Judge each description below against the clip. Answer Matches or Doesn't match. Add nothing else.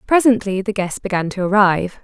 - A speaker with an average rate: Matches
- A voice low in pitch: Doesn't match